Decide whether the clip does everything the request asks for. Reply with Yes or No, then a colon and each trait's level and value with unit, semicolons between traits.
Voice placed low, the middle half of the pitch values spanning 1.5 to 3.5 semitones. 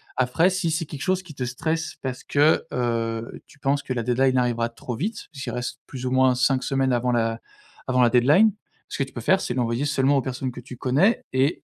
Yes: low, 130 Hz; average, 2.9 semitones